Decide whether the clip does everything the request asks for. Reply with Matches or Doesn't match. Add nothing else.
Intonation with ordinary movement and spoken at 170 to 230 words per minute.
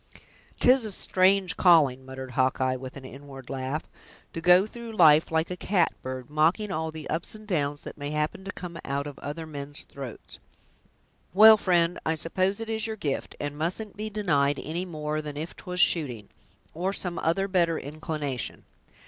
Matches